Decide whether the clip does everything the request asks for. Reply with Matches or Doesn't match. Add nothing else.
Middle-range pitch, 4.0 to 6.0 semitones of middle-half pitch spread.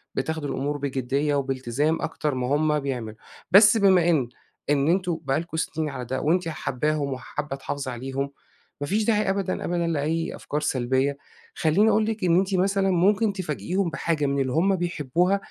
Matches